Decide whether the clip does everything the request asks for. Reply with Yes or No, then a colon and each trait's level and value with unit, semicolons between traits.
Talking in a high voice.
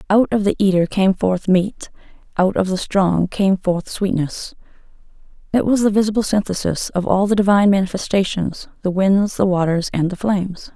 Yes: high, 195 Hz